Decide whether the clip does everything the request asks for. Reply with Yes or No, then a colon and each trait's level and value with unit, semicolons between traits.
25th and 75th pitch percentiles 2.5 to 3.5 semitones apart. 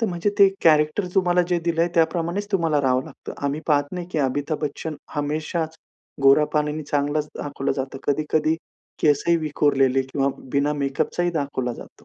Yes: average, 2.9 semitones